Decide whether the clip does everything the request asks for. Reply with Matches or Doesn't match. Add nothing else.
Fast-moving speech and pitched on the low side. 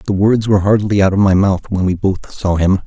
Matches